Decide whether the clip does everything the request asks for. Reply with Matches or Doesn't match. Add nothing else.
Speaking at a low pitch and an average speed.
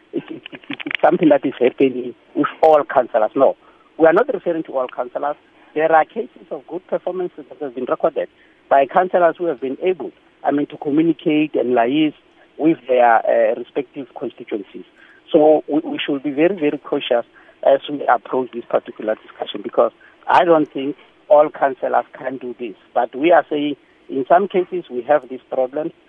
Doesn't match